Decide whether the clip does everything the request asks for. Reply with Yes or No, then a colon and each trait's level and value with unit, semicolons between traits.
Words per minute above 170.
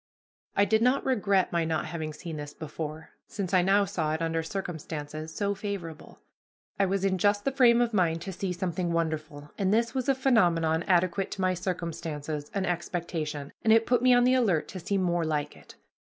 Yes: average, 200 wpm